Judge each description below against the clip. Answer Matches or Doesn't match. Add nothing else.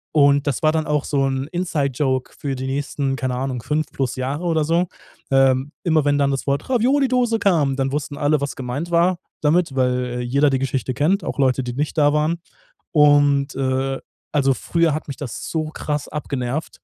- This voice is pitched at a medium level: Matches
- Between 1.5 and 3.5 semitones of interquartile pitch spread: Matches